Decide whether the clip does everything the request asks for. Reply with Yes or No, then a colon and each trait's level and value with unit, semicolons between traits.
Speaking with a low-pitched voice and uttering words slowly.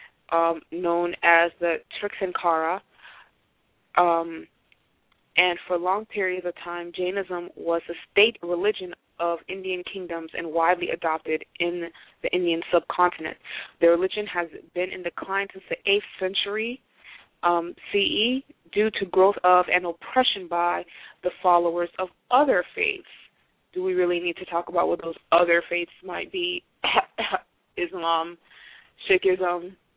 No: medium, 175 Hz; slow, 130 wpm